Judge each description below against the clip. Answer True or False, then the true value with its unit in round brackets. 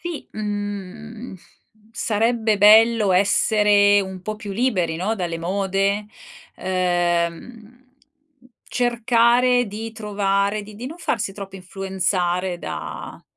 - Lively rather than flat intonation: False (2.9 semitones)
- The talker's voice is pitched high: True (205 Hz)